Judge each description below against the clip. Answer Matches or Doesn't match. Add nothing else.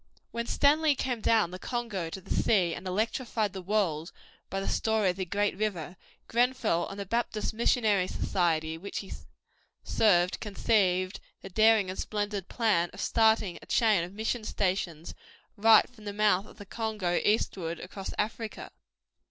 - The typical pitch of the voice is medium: Doesn't match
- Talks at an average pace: Matches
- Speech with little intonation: Doesn't match